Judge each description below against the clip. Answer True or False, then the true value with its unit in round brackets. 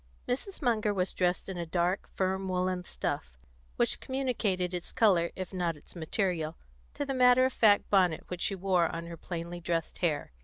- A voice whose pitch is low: False (185 Hz)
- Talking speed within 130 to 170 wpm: False (185 wpm)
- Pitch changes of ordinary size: True (3.1 semitones)